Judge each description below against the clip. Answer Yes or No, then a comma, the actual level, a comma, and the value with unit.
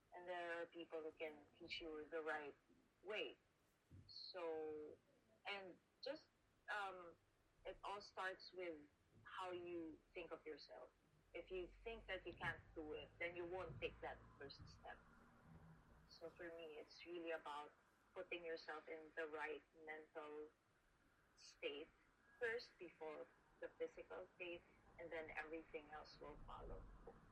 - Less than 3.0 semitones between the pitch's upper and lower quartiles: Yes, narrow, 2.5 semitones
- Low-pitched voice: No, medium, 165 Hz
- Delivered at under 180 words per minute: Yes, average, 140 wpm